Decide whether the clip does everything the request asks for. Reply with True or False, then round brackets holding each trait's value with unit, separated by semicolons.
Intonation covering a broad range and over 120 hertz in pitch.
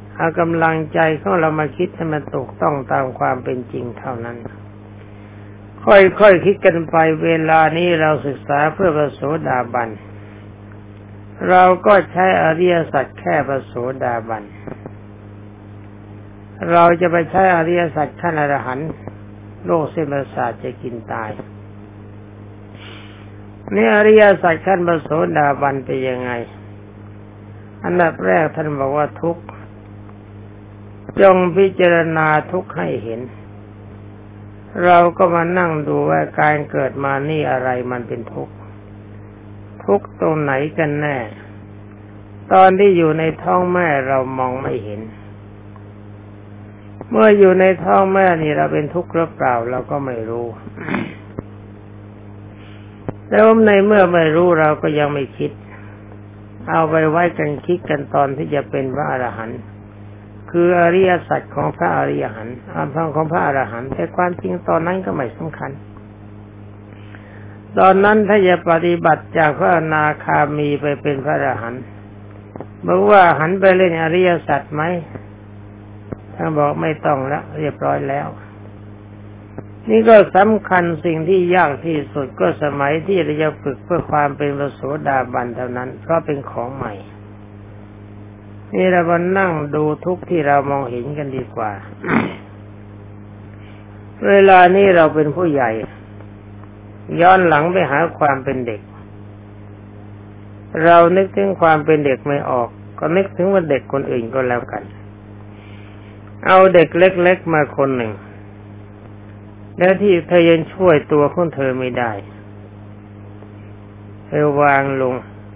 True (7.9 semitones; 130 Hz)